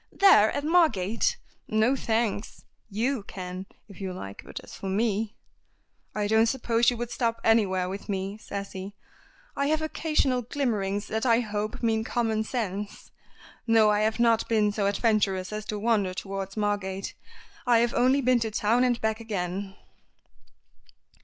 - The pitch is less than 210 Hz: No, high, 220 Hz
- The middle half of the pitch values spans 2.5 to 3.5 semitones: Yes, average, 2.9 semitones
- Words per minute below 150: No, average, 160 wpm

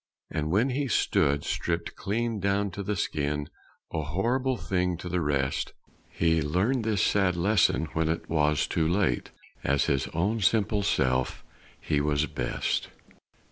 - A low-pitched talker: Yes, very low, 85 Hz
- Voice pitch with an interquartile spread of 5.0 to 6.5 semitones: Yes, average, 5.3 semitones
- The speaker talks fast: No, average, 150 wpm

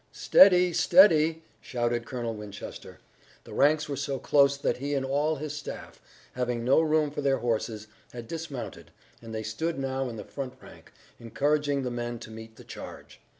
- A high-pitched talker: No, low, 135 Hz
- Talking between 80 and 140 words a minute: No, average, 180 wpm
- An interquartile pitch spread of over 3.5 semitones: Yes, average, 4.0 semitones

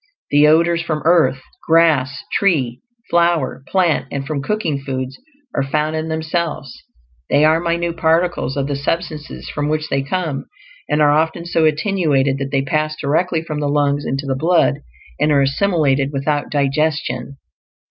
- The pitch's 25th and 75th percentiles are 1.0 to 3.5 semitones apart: Yes, average, 3.0 semitones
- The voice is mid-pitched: Yes, medium, 150 Hz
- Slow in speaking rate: No, average, 160 wpm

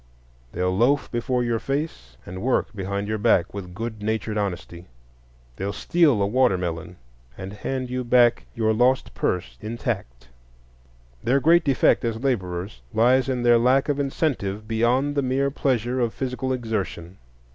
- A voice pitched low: Yes, low, 115 Hz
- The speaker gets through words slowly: No, average, 150 wpm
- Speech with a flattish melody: No, average, 4.7 semitones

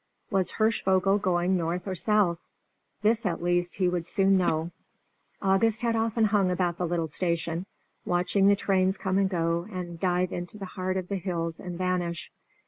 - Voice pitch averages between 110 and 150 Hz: No, medium, 185 Hz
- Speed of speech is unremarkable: Yes, average, 175 wpm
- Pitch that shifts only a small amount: Yes, narrow, 2.0 semitones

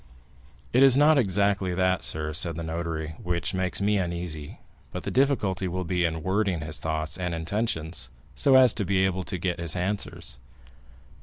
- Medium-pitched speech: No, very low, 90 Hz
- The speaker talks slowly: No, average, 175 wpm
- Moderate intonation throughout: Yes, average, 3.5 semitones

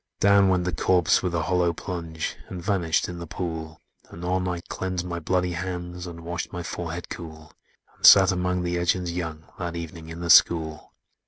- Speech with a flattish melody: Yes, narrow, 1.4 semitones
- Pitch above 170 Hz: No, very low, 85 Hz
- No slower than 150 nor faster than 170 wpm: No, average, 185 wpm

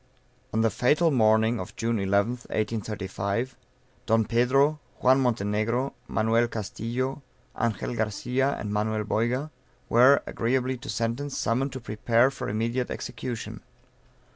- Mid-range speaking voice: No, low, 115 Hz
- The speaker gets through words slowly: Yes, slow, 120 wpm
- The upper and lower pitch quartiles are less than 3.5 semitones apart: Yes, average, 2.9 semitones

